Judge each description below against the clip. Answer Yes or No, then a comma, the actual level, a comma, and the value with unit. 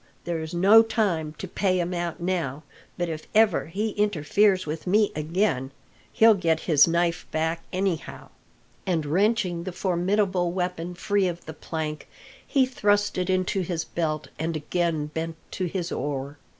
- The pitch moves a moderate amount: Yes, average, 3.2 semitones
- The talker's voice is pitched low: No, medium, 175 Hz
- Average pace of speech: Yes, average, 155 wpm